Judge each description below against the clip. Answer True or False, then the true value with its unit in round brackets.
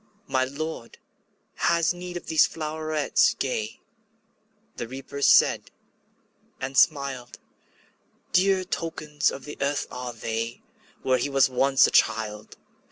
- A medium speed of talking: False (120 wpm)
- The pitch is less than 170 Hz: True (140 Hz)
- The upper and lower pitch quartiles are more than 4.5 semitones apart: False (3.8 semitones)